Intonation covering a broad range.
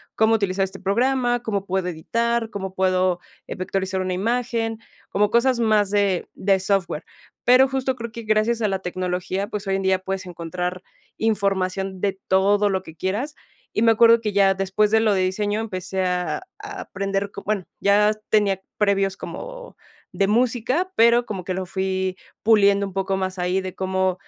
No: average, 2.9 semitones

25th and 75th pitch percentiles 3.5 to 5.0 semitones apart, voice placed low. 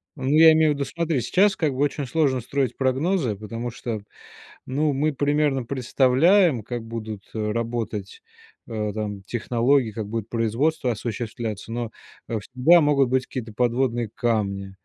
Yes: average, 4.2 semitones; low, 120 Hz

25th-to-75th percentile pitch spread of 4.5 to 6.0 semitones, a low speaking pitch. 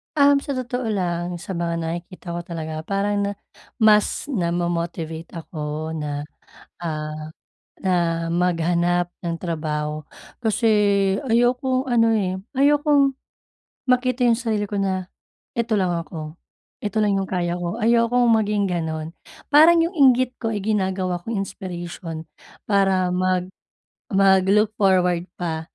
No: average, 4.8 semitones; medium, 185 Hz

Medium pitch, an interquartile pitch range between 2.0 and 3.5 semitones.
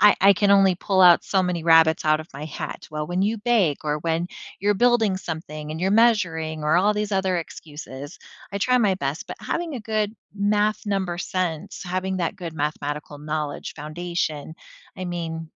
No: medium, 175 Hz; average, 4.3 semitones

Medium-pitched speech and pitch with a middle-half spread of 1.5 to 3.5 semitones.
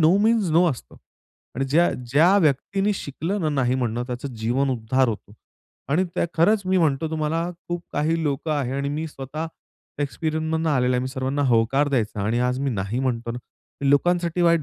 No: medium, 145 Hz; average, 4.5 semitones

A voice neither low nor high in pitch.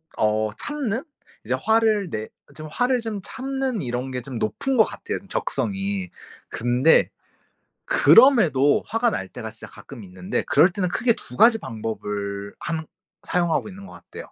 Yes: medium, 175 Hz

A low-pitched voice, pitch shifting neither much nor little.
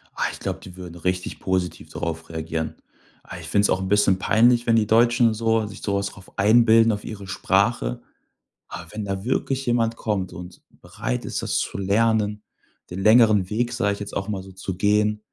Yes: low, 100 Hz; average, 3.3 semitones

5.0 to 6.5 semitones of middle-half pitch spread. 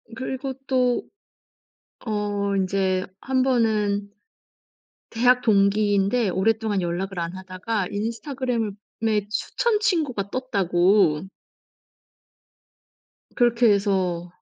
No: average, 4.0 semitones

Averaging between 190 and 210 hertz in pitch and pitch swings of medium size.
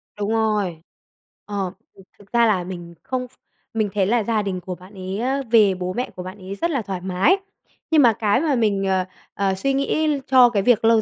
Yes: high, 205 Hz; average, 4.3 semitones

